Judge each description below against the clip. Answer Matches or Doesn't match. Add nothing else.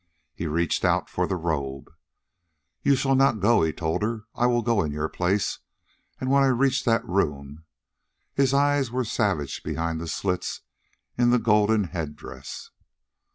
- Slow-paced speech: Doesn't match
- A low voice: Matches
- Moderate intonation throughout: Doesn't match